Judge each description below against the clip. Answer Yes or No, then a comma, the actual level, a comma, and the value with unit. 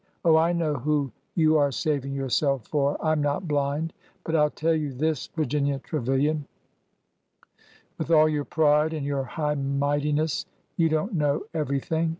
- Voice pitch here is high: No, medium, 150 Hz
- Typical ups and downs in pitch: No, narrow, 2.1 semitones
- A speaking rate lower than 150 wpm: No, average, 175 wpm